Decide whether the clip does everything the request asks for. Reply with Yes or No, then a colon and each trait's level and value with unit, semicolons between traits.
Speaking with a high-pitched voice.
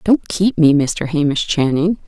No: medium, 160 Hz